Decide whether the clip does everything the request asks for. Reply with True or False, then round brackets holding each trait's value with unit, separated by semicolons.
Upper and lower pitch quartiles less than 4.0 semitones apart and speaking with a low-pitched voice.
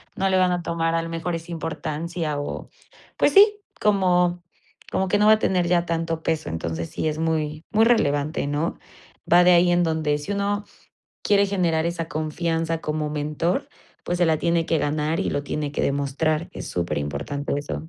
False (2.7 semitones; 165 Hz)